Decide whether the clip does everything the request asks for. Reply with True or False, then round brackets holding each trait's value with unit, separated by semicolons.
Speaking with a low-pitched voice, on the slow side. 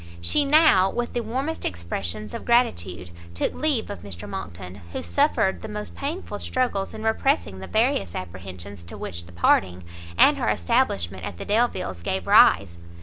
False (95 Hz; 165 wpm)